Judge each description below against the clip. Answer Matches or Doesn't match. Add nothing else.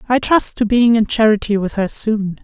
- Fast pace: Matches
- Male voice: Doesn't match